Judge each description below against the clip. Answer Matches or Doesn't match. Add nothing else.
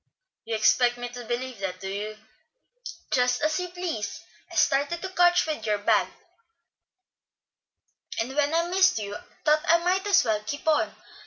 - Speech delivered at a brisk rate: Doesn't match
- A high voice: Matches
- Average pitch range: Doesn't match